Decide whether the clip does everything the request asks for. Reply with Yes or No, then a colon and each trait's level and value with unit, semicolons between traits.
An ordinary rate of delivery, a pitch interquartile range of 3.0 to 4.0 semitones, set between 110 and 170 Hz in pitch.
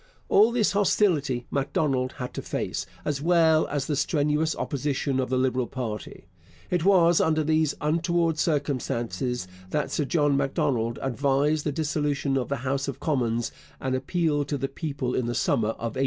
Yes: average, 170 wpm; average, 3.4 semitones; medium, 140 Hz